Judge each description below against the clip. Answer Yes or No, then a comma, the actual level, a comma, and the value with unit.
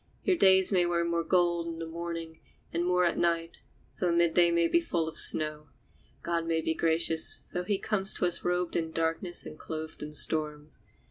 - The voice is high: No, medium, 170 Hz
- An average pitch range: No, narrow, 1.5 semitones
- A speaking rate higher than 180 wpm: Yes, average, 195 wpm